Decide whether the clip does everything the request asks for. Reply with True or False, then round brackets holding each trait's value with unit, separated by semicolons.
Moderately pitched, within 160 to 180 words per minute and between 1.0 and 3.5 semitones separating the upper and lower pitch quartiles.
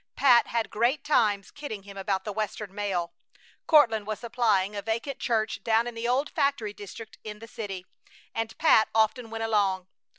False (220 Hz; 175 wpm; 2.6 semitones)